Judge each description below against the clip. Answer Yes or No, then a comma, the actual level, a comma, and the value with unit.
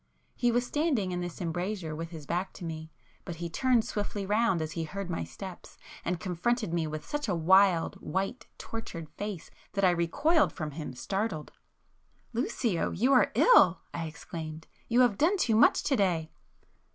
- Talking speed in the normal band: Yes, average, 175 wpm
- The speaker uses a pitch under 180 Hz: No, medium, 185 Hz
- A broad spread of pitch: Yes, wide, 5.7 semitones